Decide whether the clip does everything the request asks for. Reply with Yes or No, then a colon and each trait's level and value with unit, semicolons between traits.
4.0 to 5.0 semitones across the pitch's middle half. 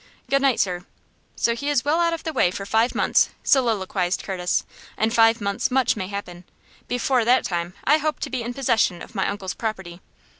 No: wide, 5.5 semitones